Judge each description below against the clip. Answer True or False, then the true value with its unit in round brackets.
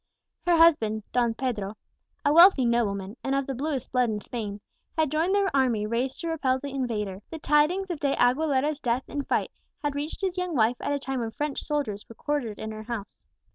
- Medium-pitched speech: False (265 Hz)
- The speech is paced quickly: True (210 wpm)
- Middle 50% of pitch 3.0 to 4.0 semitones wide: False (4.7 semitones)